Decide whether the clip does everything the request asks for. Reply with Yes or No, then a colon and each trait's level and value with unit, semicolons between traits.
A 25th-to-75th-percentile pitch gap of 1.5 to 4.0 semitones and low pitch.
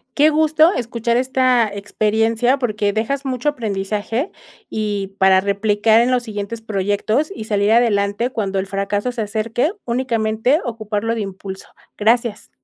No: average, 3.2 semitones; high, 220 Hz